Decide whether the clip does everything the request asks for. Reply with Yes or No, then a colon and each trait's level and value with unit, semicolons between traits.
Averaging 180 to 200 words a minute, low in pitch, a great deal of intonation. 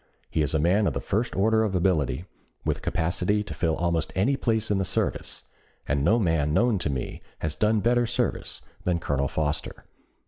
Yes: average, 195 wpm; very low, 90 Hz; wide, 5.9 semitones